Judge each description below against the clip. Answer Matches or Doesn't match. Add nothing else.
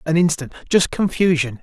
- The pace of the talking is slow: Matches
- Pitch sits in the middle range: Matches